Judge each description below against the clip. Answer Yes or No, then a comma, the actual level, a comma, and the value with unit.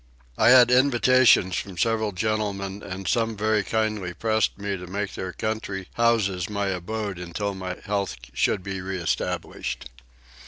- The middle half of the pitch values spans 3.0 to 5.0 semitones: No, narrow, 2.6 semitones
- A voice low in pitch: Yes, low, 100 Hz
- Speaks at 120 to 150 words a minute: Yes, average, 145 wpm